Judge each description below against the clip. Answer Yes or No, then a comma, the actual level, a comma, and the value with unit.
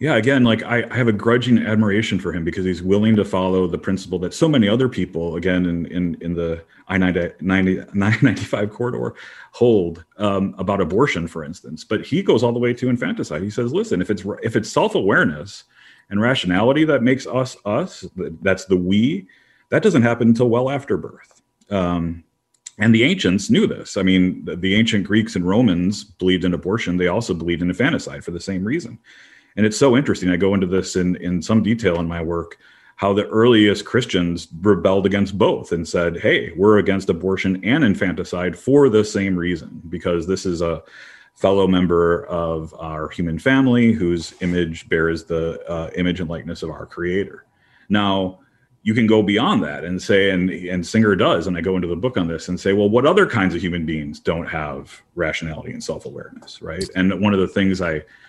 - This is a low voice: Yes, very low, 95 Hz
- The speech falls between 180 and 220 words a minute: Yes, average, 200 wpm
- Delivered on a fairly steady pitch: No, average, 3.7 semitones